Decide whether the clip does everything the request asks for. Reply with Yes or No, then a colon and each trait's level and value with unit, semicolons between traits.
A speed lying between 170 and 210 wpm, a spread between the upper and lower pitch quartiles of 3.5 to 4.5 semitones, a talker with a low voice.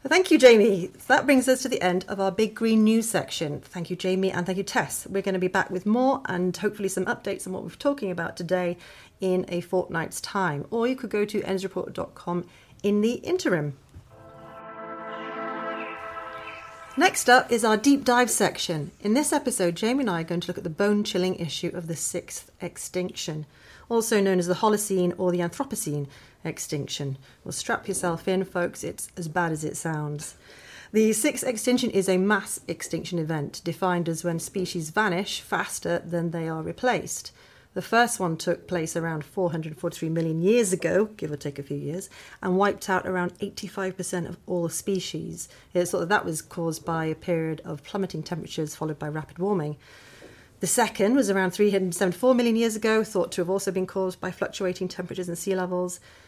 No: average, 190 wpm; average, 3.8 semitones; medium, 185 Hz